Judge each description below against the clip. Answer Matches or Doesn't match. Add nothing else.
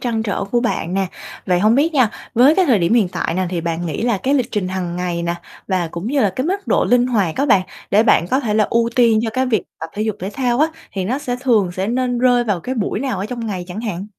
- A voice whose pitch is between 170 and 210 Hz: Doesn't match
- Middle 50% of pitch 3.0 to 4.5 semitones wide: Doesn't match